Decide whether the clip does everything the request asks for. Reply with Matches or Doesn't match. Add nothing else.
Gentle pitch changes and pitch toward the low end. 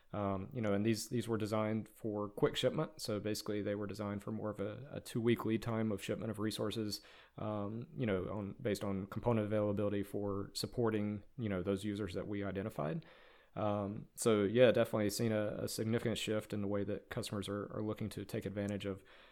Matches